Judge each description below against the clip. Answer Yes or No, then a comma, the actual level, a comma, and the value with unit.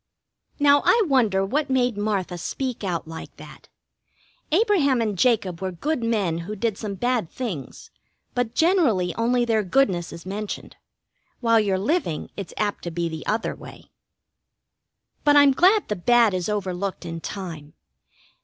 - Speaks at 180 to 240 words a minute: No, average, 155 wpm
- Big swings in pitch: Yes, wide, 5.7 semitones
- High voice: Yes, high, 215 Hz